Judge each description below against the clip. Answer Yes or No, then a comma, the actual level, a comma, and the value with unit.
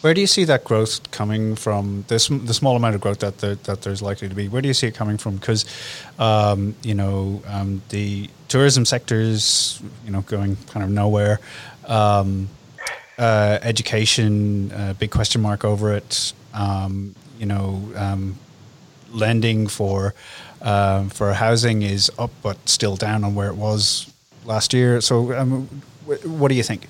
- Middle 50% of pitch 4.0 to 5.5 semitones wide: No, average, 3.1 semitones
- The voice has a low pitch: Yes, low, 110 Hz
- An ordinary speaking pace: Yes, average, 170 wpm